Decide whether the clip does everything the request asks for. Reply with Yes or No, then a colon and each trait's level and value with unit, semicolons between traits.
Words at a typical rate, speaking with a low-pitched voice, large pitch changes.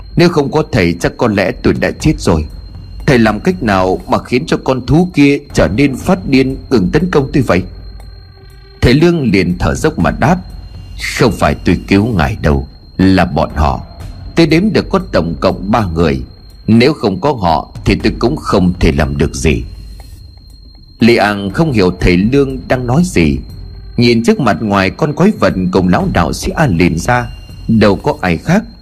Yes: average, 195 wpm; very low, 95 Hz; wide, 6.9 semitones